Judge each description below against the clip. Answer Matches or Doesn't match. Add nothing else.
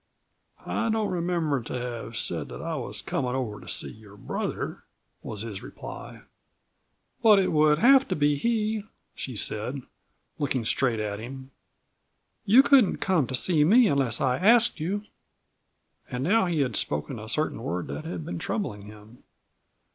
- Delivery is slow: Doesn't match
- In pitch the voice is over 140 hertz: Doesn't match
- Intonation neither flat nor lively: Doesn't match